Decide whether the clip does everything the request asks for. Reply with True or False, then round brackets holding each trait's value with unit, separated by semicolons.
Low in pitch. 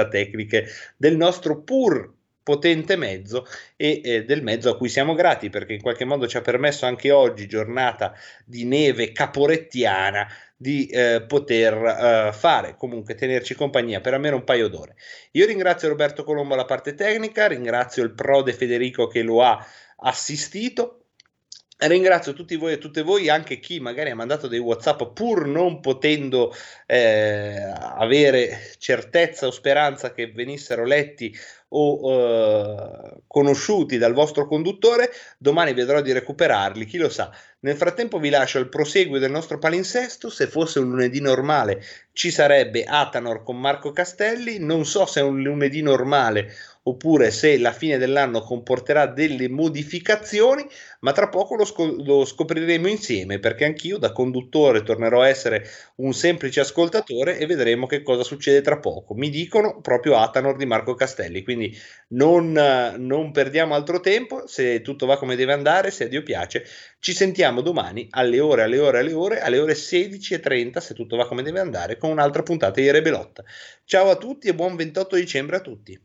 False (145 Hz)